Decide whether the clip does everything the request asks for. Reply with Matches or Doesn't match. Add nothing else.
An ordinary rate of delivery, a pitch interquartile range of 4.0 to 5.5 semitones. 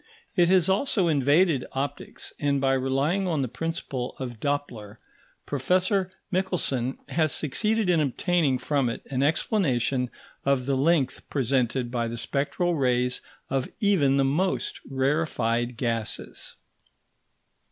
Doesn't match